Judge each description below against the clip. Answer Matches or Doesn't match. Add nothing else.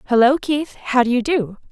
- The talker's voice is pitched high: Matches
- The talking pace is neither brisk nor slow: Doesn't match